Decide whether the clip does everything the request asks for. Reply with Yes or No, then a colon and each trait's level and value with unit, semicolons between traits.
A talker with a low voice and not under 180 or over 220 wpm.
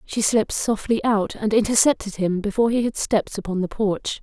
No: high, 210 Hz; average, 200 wpm